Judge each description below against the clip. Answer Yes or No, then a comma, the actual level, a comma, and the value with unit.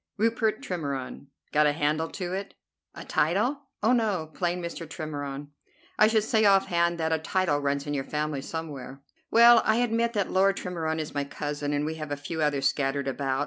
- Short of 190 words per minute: No, average, 195 wpm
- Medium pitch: Yes, medium, 160 Hz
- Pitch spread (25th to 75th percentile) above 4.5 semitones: Yes, average, 5.3 semitones